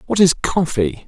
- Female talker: No, male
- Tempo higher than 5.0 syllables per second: No, 4.4 syllables/s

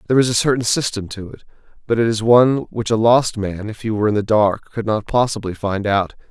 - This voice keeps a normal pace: No, fast, 245 wpm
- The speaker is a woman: No, male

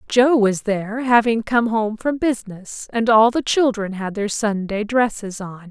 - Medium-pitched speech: No, high, 220 Hz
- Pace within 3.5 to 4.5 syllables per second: Yes, 4.4 syllables/s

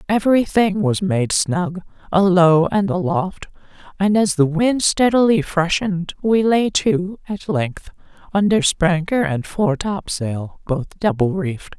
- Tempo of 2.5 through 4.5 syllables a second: Yes, 4.0 syllables/s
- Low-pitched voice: No, medium, 185 Hz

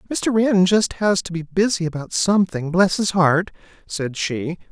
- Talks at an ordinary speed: Yes, average, 180 wpm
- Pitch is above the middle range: No, medium, 180 Hz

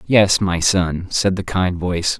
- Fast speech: No, average, 190 wpm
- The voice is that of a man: Yes, male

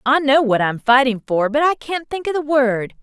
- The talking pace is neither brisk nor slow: No, fast, 260 wpm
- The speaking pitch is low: No, very high, 265 Hz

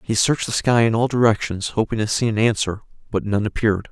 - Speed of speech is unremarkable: No, fast, 230 wpm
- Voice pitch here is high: No, low, 110 Hz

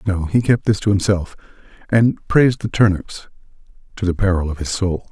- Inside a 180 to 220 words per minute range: Yes, average, 190 wpm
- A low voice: Yes, low, 100 Hz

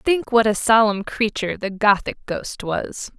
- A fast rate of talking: No, average, 170 wpm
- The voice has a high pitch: Yes, high, 215 Hz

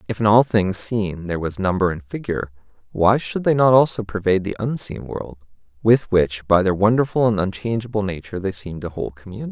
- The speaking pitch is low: Yes, low, 105 Hz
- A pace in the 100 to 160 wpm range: No, average, 200 wpm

